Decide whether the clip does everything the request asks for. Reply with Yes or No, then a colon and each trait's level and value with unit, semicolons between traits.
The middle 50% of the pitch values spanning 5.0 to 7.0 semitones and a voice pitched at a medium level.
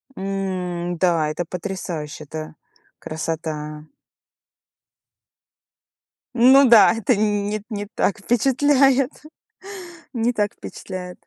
No: wide, 5.5 semitones; high, 195 Hz